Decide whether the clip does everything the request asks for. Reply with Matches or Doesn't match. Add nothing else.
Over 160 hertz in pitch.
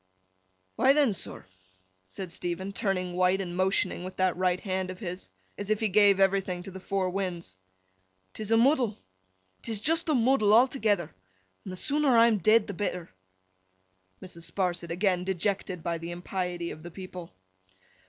Matches